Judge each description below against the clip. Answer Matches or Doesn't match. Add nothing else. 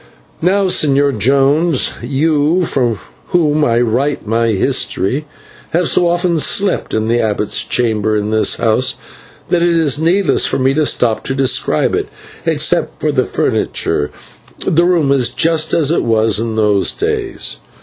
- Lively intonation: Matches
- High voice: Doesn't match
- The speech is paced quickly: Doesn't match